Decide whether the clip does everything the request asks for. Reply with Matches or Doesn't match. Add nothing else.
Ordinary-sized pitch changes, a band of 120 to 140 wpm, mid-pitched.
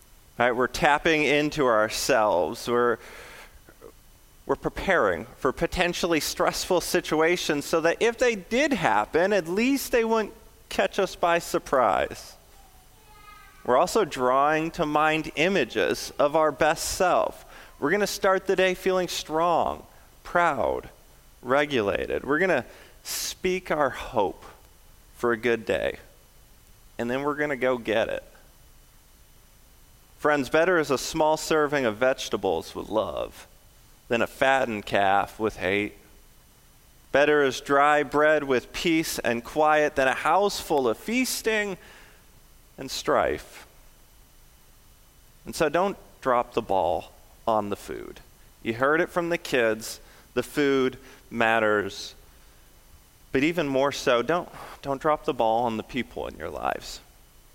Doesn't match